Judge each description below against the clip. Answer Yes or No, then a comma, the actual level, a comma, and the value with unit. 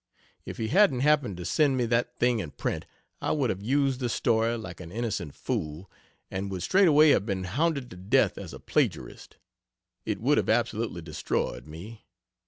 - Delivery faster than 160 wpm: Yes, average, 185 wpm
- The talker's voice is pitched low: Yes, low, 115 Hz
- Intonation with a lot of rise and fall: Yes, wide, 6.1 semitones